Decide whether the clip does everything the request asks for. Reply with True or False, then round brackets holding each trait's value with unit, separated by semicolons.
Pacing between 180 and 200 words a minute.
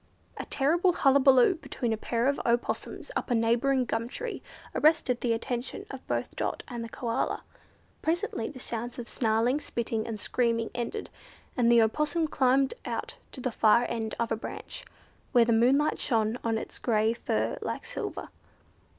False (165 wpm)